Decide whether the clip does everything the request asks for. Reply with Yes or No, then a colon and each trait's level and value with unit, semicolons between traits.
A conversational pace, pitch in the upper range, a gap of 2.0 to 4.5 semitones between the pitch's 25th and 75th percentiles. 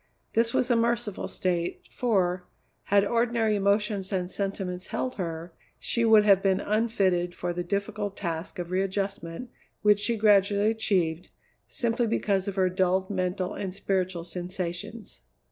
Yes: average, 145 wpm; high, 195 Hz; average, 2.9 semitones